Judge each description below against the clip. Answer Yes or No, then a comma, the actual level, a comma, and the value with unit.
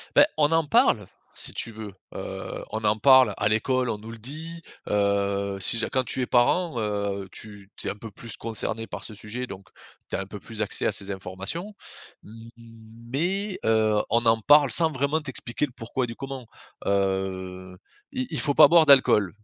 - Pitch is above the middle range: No, low, 115 Hz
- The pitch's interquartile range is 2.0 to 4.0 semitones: No, wide, 5.5 semitones